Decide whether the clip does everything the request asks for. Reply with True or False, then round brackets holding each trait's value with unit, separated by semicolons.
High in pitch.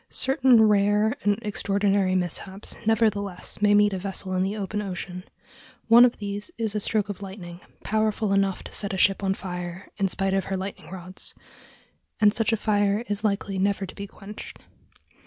True (200 Hz)